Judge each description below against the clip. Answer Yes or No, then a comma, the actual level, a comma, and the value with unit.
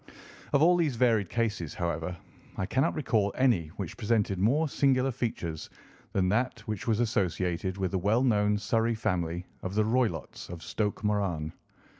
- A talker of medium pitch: No, low, 105 Hz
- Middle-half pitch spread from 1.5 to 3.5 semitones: No, average, 4.6 semitones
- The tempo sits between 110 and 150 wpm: No, average, 160 wpm